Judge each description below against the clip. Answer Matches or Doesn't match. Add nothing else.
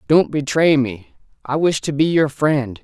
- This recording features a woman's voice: Doesn't match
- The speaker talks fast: Doesn't match